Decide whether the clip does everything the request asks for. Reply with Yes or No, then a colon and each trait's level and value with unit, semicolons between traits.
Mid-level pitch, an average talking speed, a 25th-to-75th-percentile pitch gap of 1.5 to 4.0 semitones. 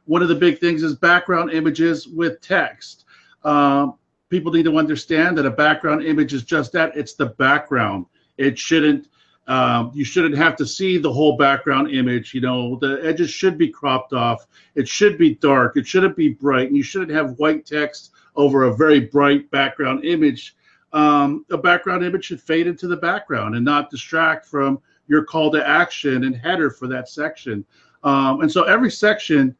Yes: medium, 150 Hz; average, 185 wpm; average, 3.2 semitones